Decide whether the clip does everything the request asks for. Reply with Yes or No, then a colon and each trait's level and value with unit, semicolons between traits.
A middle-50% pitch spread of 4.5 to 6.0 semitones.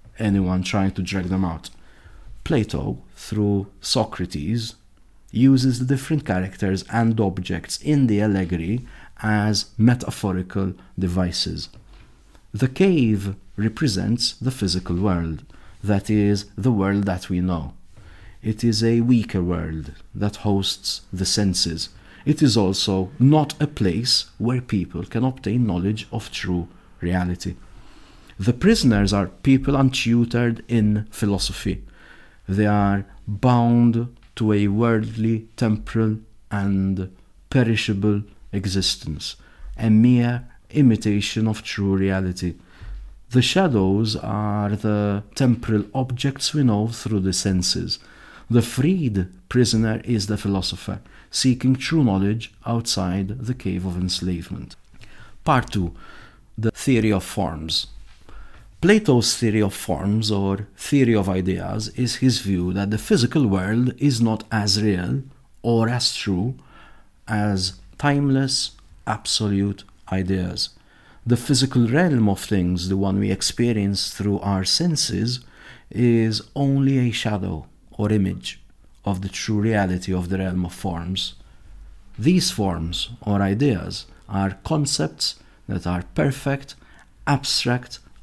No: average, 4.0 semitones